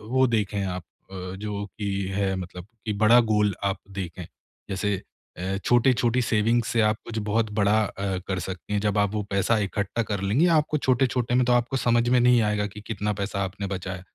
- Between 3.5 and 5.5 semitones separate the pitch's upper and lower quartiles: No, average, 2.9 semitones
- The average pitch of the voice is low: Yes, low, 105 Hz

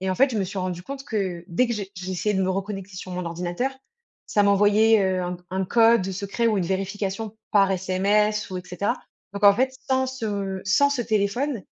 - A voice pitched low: No, high, 200 Hz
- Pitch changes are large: No, average, 2.9 semitones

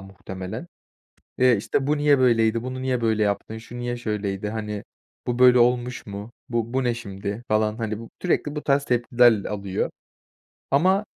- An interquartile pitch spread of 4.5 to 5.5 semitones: No, average, 3.2 semitones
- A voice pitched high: No, low, 120 Hz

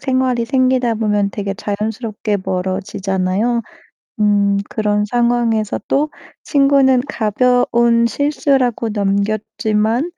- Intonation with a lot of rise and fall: No, average, 3.4 semitones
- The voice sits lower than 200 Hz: No, high, 225 Hz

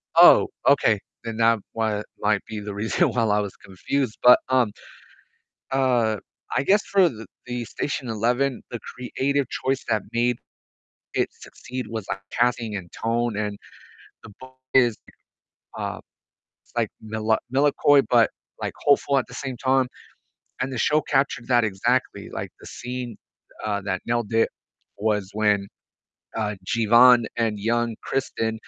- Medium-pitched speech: No, low, 115 Hz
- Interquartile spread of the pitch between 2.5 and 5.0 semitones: Yes, average, 3.1 semitones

